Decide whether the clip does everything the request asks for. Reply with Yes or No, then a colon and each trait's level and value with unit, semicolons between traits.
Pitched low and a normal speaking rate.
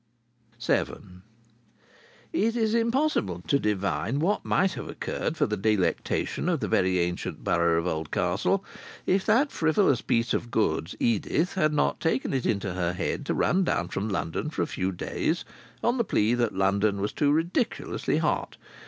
Yes: low, 115 Hz; average, 165 wpm